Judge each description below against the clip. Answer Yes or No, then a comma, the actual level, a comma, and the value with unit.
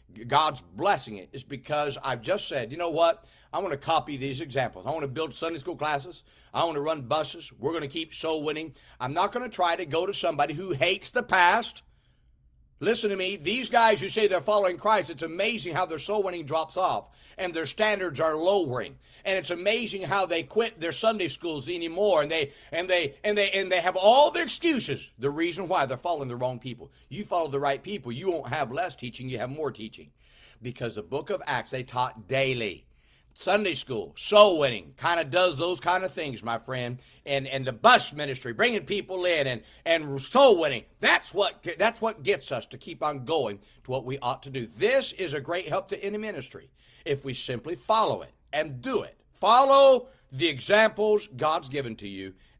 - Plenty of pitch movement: Yes, wide, 6.1 semitones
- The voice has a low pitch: No, medium, 165 Hz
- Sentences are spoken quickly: Yes, fast, 215 wpm